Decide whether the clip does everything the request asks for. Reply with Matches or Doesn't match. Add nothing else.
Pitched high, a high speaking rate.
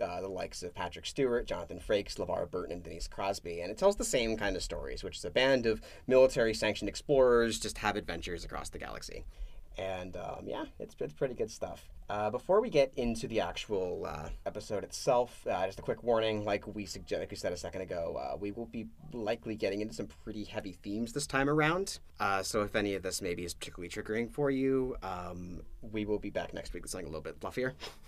Doesn't match